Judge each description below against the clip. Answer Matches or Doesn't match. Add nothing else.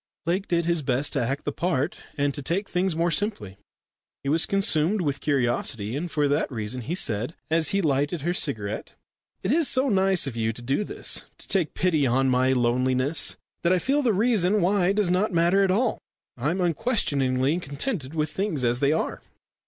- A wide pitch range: Matches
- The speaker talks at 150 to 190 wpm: Doesn't match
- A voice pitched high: Doesn't match